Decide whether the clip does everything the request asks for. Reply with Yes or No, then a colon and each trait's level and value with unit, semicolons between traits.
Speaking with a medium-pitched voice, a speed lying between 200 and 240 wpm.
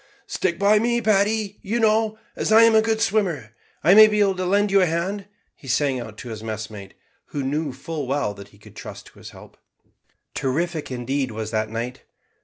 Yes: medium, 165 Hz; fast, 205 wpm